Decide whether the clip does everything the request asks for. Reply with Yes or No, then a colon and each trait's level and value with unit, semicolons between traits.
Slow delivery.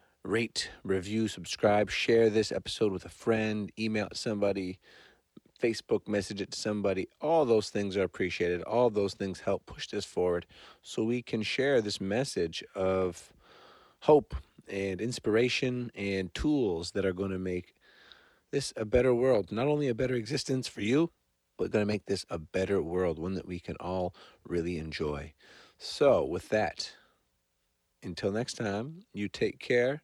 No: average, 160 wpm